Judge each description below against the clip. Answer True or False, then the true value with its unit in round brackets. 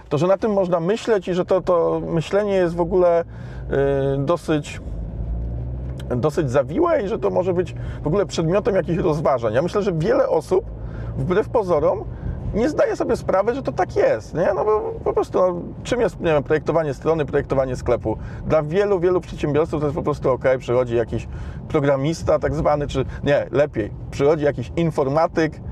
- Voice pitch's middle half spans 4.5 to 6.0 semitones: True (5.1 semitones)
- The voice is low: False (155 Hz)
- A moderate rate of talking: False (175 wpm)